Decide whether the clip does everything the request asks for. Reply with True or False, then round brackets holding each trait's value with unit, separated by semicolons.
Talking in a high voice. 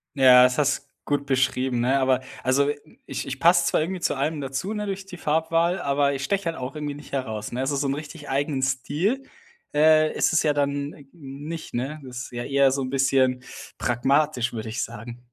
False (140 Hz)